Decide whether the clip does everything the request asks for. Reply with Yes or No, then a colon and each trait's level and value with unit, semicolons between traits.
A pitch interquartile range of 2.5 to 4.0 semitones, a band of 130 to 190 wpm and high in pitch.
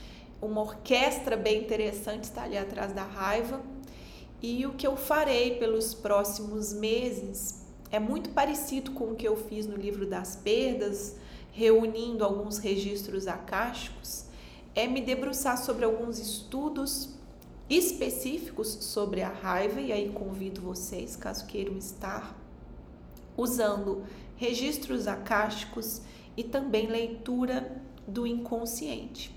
No: average, 3.5 semitones; slow, 120 wpm; high, 220 Hz